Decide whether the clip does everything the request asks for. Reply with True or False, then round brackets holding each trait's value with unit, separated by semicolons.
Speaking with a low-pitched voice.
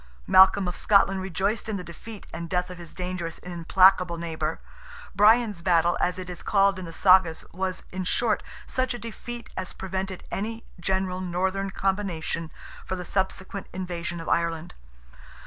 False (185 Hz)